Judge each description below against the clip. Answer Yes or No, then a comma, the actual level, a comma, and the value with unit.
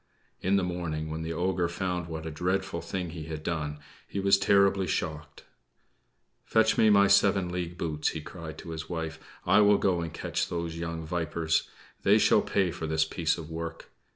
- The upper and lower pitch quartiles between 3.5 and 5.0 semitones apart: No, average, 2.8 semitones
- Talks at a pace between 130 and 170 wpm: No, average, 190 wpm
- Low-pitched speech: Yes, very low, 85 Hz